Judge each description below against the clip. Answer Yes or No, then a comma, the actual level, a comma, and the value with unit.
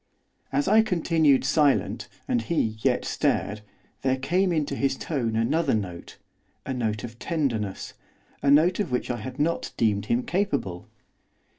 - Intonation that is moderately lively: No, wide, 6.4 semitones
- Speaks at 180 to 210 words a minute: No, average, 150 wpm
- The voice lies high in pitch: No, low, 135 Hz